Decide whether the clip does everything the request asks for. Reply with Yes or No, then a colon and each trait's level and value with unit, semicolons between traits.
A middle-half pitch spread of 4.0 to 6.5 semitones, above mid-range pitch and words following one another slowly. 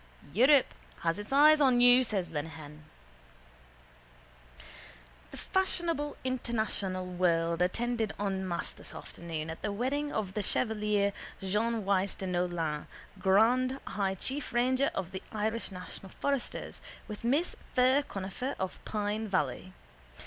Yes: wide, 5.4 semitones; high, 210 Hz; slow, 125 wpm